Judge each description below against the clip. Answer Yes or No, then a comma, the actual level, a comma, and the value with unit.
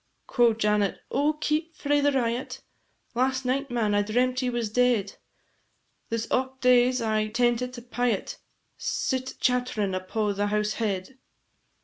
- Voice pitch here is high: Yes, high, 245 Hz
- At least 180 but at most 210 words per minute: No, average, 140 wpm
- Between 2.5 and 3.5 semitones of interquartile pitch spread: Yes, average, 3.2 semitones